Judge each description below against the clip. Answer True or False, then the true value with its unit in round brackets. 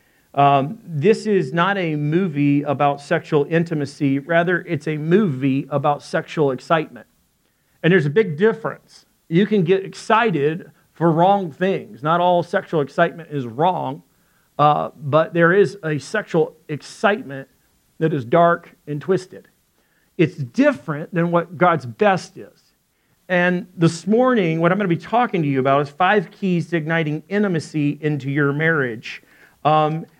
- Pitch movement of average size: True (4.1 semitones)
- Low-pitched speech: False (165 Hz)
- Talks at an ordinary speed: True (150 wpm)